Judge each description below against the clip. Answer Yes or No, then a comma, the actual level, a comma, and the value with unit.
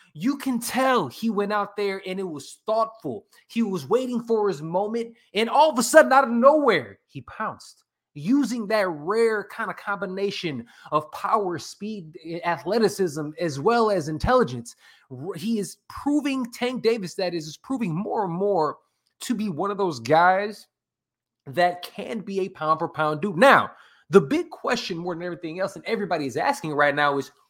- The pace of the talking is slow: No, average, 180 wpm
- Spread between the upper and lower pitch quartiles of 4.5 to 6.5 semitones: Yes, average, 5.3 semitones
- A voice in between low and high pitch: No, high, 200 Hz